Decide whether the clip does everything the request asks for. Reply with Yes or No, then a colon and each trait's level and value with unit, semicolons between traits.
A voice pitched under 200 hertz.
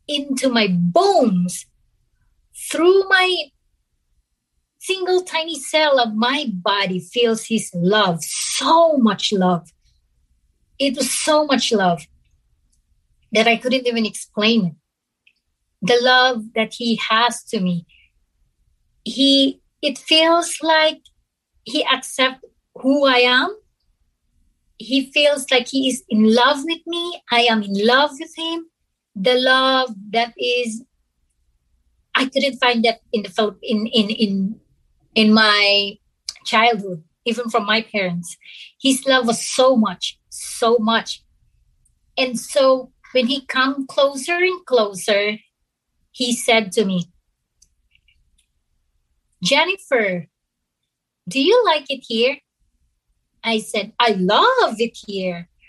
No: high, 235 Hz